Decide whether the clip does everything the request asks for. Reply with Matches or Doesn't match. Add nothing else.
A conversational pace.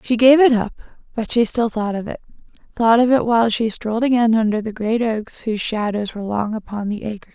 Doesn't match